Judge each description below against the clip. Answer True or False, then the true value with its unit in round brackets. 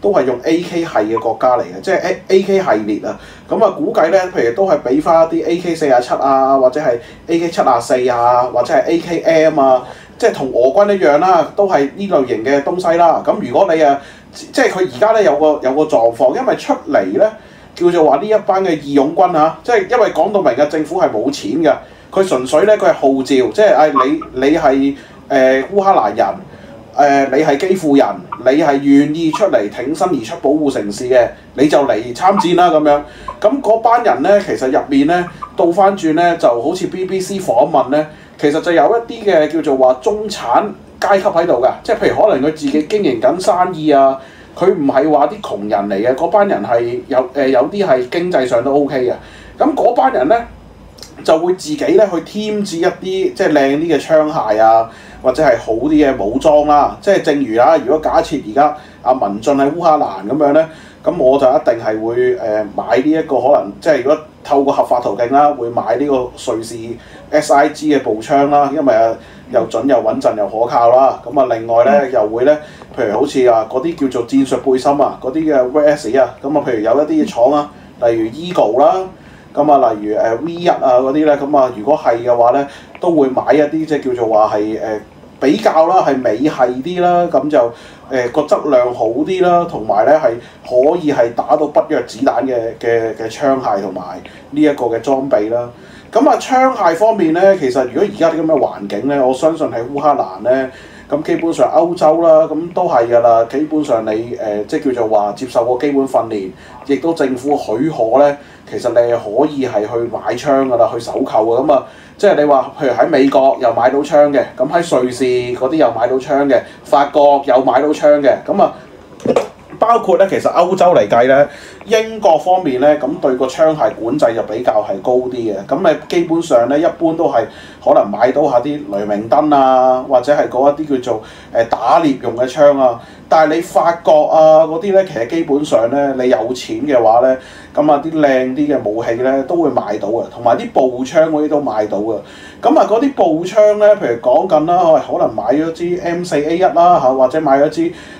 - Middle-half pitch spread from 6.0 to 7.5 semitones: False (5.3 semitones)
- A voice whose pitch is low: False (150 Hz)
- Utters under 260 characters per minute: False (300 characters per minute)